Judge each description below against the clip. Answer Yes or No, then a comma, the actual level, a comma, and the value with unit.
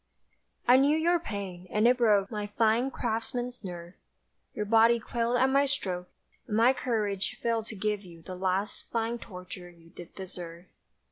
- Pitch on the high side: Yes, high, 215 Hz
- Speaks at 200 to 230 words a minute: No, average, 165 wpm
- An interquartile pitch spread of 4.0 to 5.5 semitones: Yes, average, 4.4 semitones